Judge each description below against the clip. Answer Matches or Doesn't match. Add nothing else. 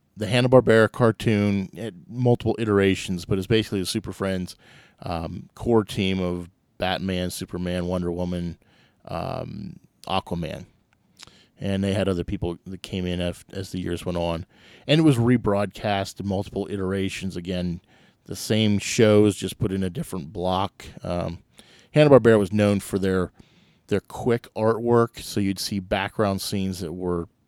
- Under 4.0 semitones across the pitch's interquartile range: Matches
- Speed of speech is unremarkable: Matches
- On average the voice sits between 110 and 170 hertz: Doesn't match